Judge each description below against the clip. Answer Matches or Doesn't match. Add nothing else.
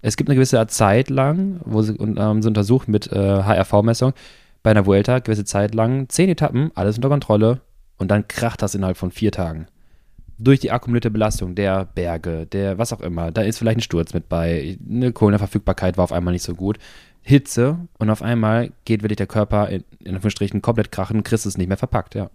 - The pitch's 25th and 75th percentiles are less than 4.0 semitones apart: Matches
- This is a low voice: Matches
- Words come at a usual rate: Doesn't match